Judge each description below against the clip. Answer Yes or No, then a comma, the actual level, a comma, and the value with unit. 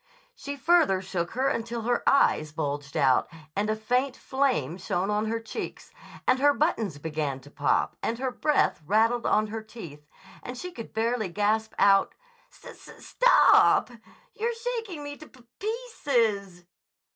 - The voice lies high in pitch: Yes, high, 225 Hz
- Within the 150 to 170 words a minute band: Yes, average, 165 wpm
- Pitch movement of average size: No, wide, 6.4 semitones